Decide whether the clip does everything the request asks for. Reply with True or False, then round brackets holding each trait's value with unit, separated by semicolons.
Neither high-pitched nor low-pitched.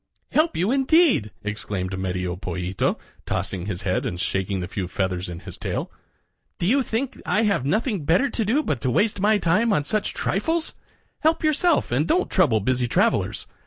True (145 Hz)